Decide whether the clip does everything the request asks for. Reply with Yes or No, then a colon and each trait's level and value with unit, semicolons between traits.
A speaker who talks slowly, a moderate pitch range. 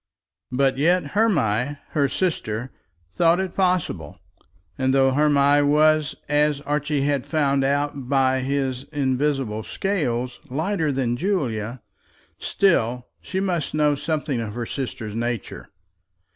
Yes: slow, 120 wpm; average, 3.3 semitones